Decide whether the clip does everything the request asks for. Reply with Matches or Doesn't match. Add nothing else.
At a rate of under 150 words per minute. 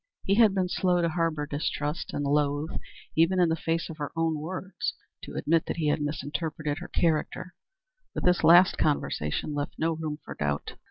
Doesn't match